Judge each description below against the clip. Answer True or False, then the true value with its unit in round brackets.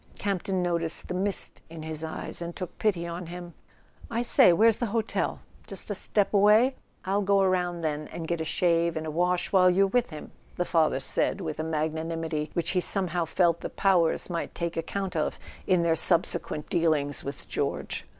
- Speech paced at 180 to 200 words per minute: True (190 wpm)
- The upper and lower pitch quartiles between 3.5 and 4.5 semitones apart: False (2.9 semitones)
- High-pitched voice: False (170 Hz)